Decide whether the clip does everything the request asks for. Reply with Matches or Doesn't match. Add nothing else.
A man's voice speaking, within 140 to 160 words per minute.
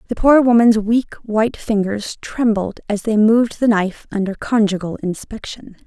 Doesn't match